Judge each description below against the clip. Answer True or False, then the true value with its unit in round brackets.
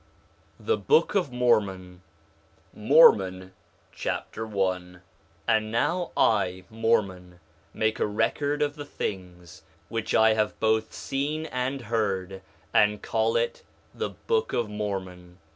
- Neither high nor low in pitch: False (110 Hz)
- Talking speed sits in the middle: False (125 wpm)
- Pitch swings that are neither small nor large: True (4.8 semitones)